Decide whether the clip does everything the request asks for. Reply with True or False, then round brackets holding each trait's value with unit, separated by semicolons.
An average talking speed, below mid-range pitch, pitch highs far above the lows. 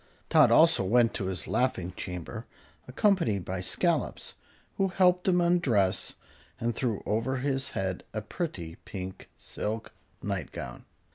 False (130 wpm; 110 Hz; 6.7 semitones)